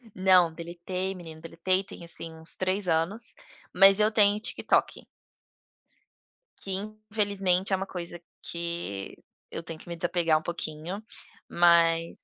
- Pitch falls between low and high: Yes, medium, 175 Hz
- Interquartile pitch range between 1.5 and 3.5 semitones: Yes, narrow, 2.5 semitones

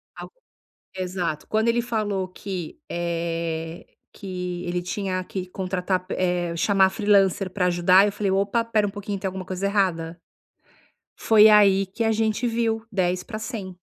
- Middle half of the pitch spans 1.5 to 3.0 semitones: Yes, narrow, 2.6 semitones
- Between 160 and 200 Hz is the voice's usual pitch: Yes, high, 190 Hz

